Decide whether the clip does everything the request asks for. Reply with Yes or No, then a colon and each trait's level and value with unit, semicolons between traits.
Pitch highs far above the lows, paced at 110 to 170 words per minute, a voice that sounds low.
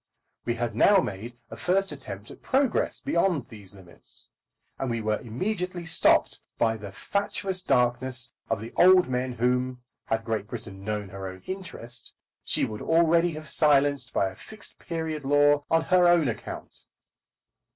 Yes: wide, 7.1 semitones; average, 160 wpm; low, 130 Hz